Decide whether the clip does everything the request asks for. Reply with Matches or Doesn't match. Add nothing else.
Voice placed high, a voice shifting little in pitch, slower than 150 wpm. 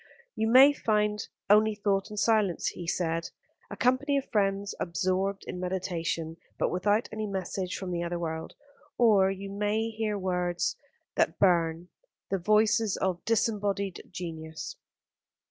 Doesn't match